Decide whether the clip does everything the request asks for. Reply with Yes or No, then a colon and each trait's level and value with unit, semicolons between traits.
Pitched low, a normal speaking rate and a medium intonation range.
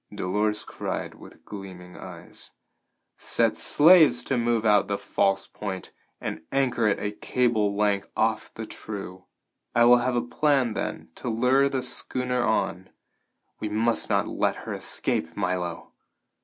Yes: low, 110 Hz; average, 145 wpm; average, 3.6 semitones